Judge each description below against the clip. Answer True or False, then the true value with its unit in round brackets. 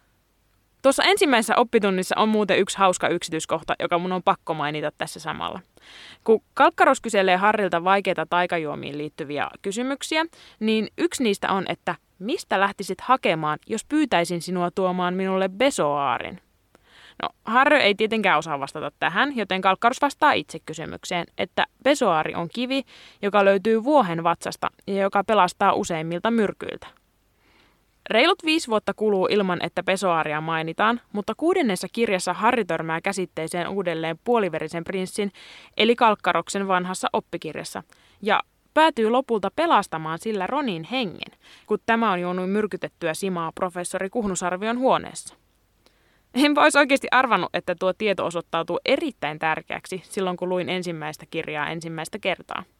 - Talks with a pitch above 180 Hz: True (190 Hz)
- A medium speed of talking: True (130 wpm)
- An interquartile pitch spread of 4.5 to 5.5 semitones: True (4.8 semitones)